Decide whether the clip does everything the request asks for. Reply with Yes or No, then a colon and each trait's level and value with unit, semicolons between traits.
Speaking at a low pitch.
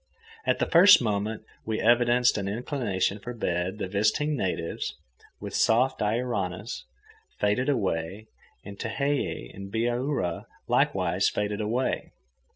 Yes: low, 110 Hz